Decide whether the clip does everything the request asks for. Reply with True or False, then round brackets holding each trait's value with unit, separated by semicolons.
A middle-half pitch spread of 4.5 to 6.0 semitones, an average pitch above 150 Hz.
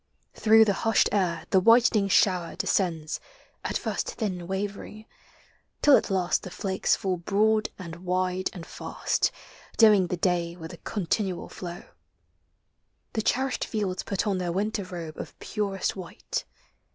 False (2.9 semitones; 190 Hz)